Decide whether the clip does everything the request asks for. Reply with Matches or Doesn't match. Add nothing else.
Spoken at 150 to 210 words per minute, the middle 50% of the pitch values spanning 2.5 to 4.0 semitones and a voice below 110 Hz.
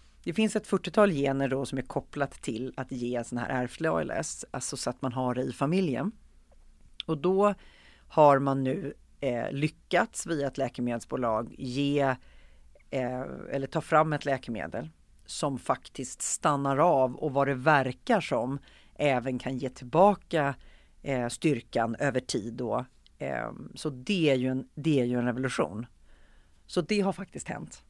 Doesn't match